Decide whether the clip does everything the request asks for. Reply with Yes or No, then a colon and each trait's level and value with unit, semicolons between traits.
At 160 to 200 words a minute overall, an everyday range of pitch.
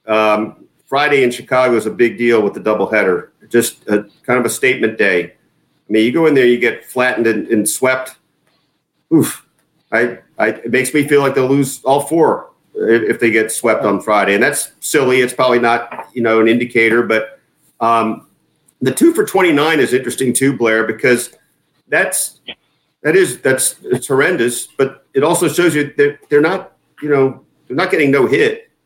Yes: average, 190 wpm; average, 4.3 semitones